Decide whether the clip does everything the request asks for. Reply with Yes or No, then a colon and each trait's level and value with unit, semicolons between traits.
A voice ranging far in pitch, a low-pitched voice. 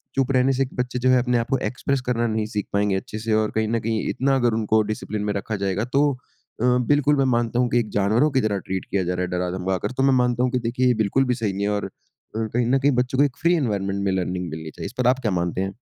No: average, 4.1 semitones; low, 115 Hz